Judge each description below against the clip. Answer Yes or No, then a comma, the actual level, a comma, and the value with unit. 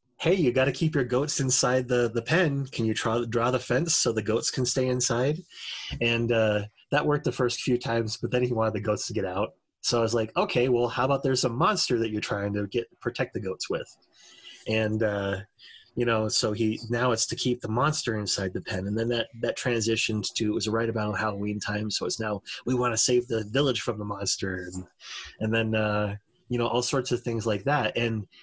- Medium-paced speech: No, fast, 235 wpm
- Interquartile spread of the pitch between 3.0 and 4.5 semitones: No, narrow, 2.5 semitones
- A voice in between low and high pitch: No, low, 115 Hz